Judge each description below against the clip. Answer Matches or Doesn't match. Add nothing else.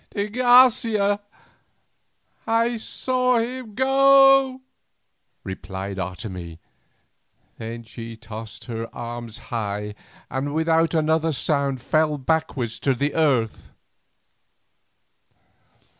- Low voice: Doesn't match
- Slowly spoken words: Matches